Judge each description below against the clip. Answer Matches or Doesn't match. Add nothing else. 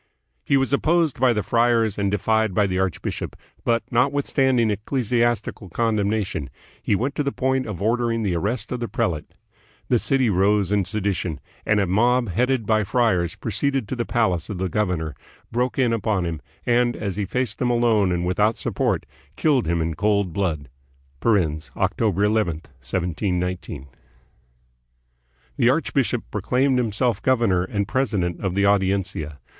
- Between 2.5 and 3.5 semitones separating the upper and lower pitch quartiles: Doesn't match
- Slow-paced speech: Doesn't match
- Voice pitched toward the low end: Matches